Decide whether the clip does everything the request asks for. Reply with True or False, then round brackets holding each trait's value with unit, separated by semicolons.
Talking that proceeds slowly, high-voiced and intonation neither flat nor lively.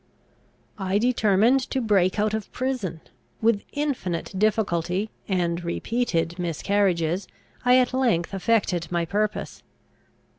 True (110 wpm; 200 Hz; 4.7 semitones)